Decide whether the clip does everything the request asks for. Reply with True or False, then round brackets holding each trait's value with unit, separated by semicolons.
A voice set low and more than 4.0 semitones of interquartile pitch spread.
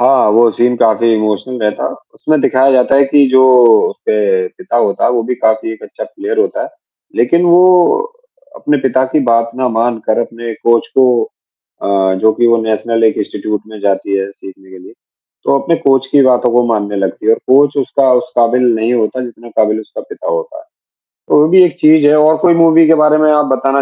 True (125 Hz; 5.1 semitones)